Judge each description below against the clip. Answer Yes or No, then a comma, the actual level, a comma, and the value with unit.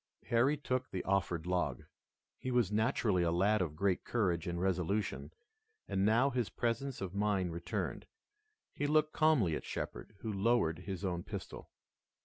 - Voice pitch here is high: No, low, 100 Hz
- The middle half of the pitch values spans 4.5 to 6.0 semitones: Yes, average, 5.2 semitones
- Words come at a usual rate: Yes, average, 155 wpm